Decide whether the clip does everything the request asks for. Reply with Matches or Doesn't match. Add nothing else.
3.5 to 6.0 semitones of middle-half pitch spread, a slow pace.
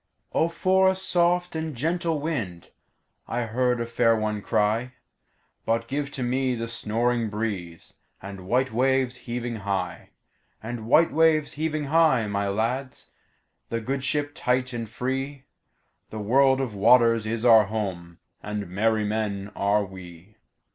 Matches